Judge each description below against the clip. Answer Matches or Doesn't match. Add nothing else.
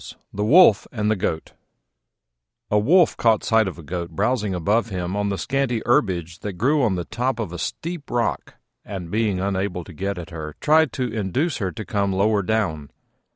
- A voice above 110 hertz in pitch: Doesn't match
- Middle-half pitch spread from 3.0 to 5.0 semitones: Matches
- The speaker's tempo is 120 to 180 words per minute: Doesn't match